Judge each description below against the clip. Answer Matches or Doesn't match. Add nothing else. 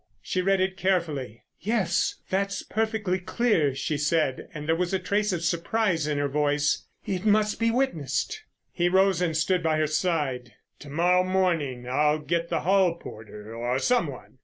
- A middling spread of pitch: Matches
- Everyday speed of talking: Matches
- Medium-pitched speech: Matches